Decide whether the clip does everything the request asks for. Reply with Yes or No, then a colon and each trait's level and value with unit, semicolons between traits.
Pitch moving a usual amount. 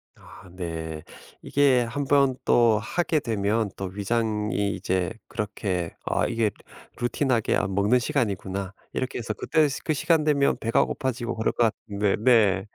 Yes: average, 4.5 semitones